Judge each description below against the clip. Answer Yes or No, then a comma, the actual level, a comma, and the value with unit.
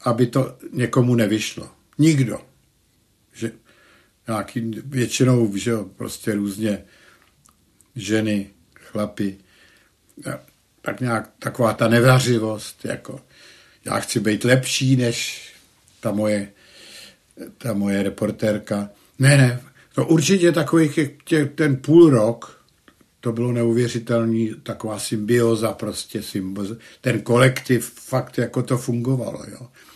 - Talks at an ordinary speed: No, slow, 105 wpm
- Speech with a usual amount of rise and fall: Yes, average, 3.1 semitones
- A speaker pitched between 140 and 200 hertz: No, low, 120 Hz